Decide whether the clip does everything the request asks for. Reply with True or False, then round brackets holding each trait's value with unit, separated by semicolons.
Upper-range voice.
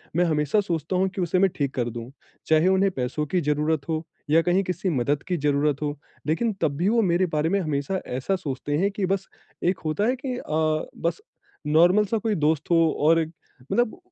False (165 Hz)